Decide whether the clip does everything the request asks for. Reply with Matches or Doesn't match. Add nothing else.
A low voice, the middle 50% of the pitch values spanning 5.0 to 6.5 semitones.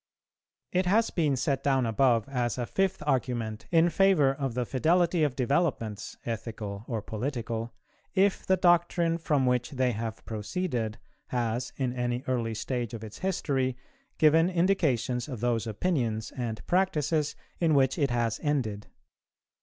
Matches